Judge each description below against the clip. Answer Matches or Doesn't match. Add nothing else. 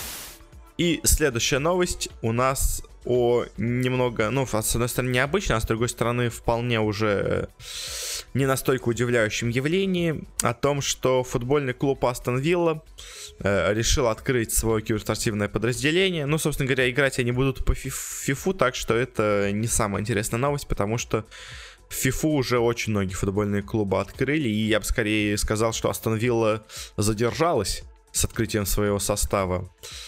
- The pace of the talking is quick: Doesn't match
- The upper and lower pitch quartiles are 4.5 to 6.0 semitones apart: Doesn't match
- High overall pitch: Doesn't match